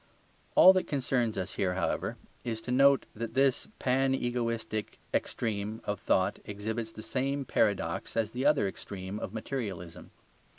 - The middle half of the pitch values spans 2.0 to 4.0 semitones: No, average, 4.4 semitones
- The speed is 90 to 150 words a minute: Yes, average, 140 wpm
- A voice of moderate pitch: No, low, 115 Hz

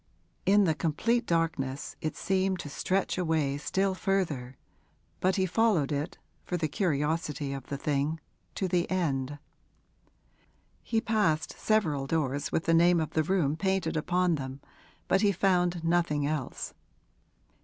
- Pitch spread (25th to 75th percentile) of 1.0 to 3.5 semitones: No, average, 4.3 semitones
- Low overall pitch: No, medium, 165 Hz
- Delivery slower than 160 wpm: Yes, average, 145 wpm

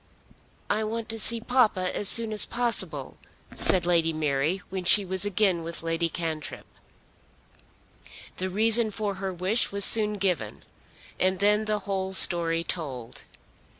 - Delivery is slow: No, average, 145 wpm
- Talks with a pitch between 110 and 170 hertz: No, high, 190 Hz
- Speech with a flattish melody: No, average, 4.0 semitones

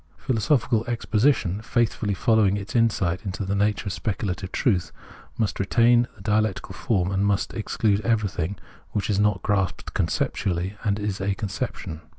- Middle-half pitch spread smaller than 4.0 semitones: Yes, narrow, 2.5 semitones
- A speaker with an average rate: Yes, average, 150 wpm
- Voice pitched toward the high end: No, low, 105 Hz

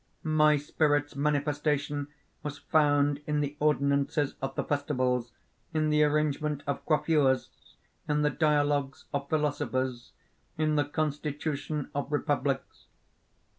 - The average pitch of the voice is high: No, medium, 145 Hz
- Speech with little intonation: Yes, narrow, 1.2 semitones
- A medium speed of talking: No, slow, 115 wpm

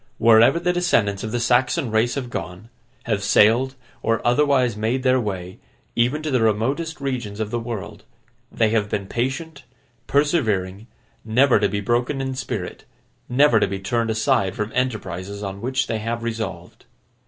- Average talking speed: Yes, average, 165 wpm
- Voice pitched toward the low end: Yes, low, 115 Hz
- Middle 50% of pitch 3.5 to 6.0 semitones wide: Yes, average, 3.8 semitones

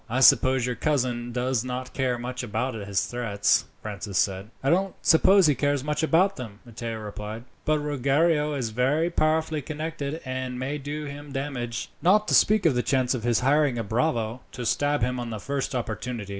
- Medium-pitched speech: No, low, 130 Hz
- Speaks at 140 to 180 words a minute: No, average, 190 wpm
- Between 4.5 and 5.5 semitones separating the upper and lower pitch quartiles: No, average, 3.9 semitones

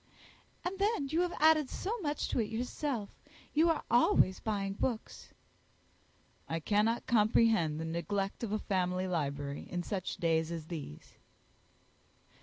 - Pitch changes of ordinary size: No, wide, 7.5 semitones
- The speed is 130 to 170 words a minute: Yes, average, 140 wpm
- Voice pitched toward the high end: Yes, high, 205 Hz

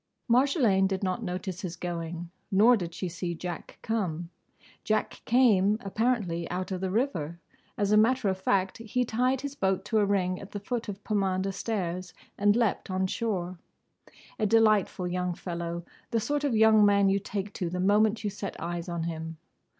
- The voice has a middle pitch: No, high, 195 Hz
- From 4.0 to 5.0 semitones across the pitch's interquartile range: No, average, 3.5 semitones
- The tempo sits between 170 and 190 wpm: Yes, average, 180 wpm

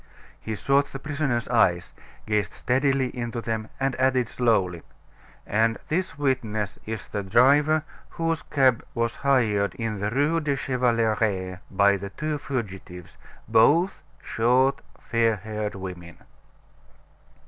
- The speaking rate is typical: No, slow, 125 wpm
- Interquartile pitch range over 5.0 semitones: No, average, 4.6 semitones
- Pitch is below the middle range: Yes, low, 115 Hz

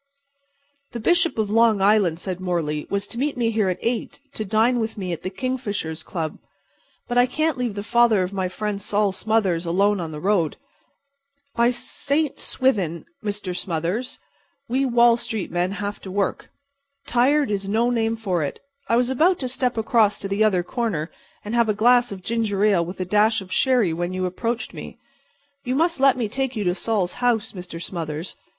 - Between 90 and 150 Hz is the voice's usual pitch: No, high, 210 Hz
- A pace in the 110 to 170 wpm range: No, average, 195 wpm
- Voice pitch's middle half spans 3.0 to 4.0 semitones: No, average, 4.5 semitones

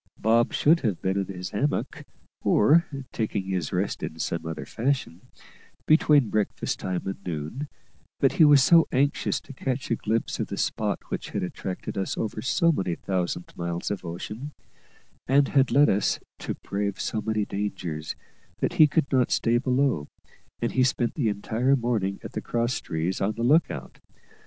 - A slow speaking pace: No, average, 175 wpm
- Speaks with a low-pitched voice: Yes, low, 110 Hz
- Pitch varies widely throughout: Yes, wide, 6.2 semitones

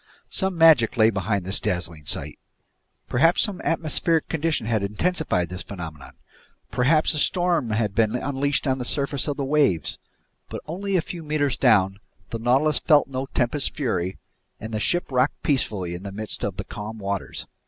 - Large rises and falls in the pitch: Yes, wide, 7.0 semitones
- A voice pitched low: Yes, low, 125 Hz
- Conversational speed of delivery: Yes, average, 175 wpm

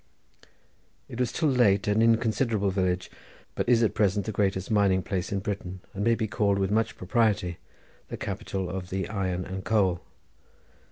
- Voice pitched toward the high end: No, low, 100 Hz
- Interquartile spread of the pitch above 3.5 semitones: No, average, 2.8 semitones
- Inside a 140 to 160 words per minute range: No, average, 170 wpm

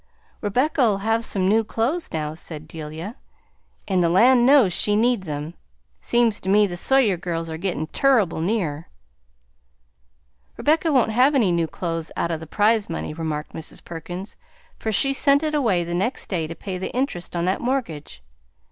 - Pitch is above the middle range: Yes, high, 195 Hz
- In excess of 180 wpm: No, average, 175 wpm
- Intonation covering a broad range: Yes, wide, 6.3 semitones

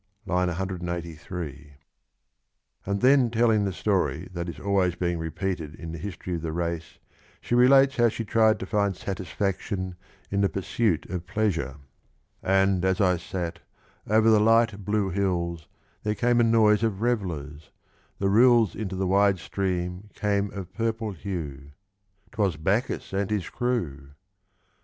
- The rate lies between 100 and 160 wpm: Yes, average, 150 wpm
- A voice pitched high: No, very low, 95 Hz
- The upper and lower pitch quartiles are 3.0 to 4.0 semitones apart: Yes, average, 3.6 semitones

